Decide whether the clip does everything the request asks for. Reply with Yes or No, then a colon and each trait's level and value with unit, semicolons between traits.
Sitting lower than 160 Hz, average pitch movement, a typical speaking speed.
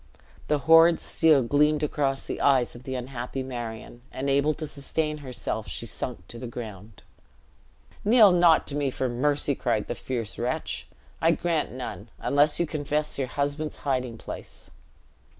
Yes: medium, 140 Hz; average, 3.5 semitones; average, 155 wpm